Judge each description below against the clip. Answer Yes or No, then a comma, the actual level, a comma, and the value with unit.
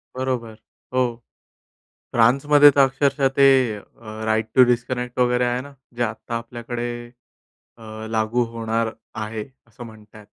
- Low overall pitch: Yes, low, 120 Hz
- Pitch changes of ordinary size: No, narrow, 2.3 semitones